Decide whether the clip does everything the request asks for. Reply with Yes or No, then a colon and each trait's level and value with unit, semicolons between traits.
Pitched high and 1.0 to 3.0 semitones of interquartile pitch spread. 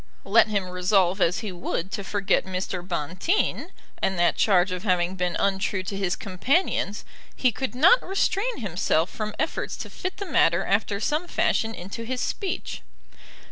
No: high, 195 Hz; average, 4.3 semitones